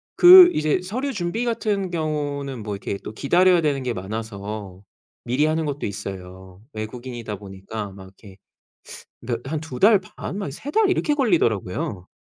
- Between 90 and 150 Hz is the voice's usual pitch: Yes, low, 135 Hz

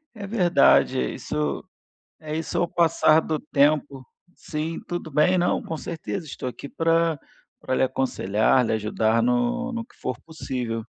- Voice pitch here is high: No, medium, 150 Hz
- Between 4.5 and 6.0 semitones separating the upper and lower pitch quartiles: Yes, average, 5.2 semitones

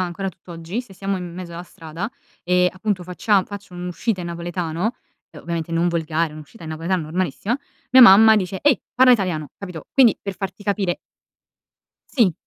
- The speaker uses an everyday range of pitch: Yes, average, 3.1 semitones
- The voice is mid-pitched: Yes, medium, 180 Hz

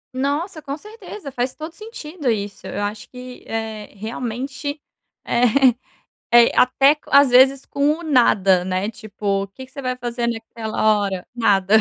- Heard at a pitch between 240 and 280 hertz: Yes, high, 245 Hz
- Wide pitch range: No, average, 4.6 semitones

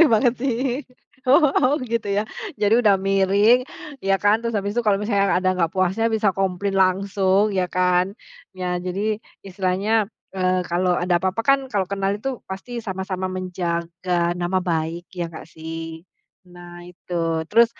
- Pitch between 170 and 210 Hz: Yes, high, 190 Hz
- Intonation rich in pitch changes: No, average, 2.9 semitones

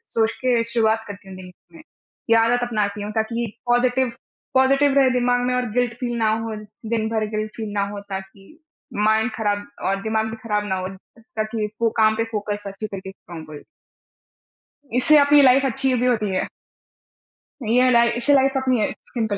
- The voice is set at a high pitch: Yes, high, 225 Hz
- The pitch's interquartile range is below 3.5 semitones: Yes, average, 3.0 semitones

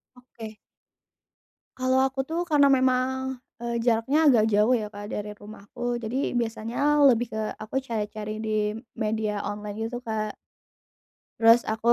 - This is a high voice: Yes, high, 225 Hz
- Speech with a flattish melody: No, average, 3.0 semitones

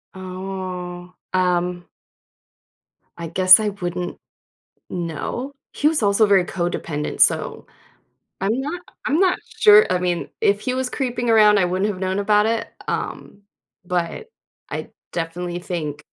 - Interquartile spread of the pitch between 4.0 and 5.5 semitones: No, average, 3.6 semitones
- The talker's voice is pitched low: No, medium, 185 Hz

